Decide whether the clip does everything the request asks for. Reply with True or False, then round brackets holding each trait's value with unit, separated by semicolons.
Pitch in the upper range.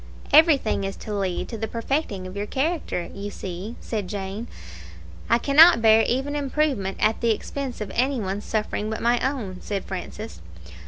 True (220 Hz)